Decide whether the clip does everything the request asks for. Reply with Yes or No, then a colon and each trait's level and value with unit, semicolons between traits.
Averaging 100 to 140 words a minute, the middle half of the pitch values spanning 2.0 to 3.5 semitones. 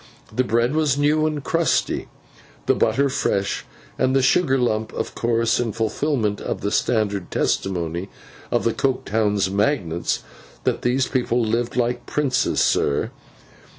No: slow, 135 wpm; average, 4.3 semitones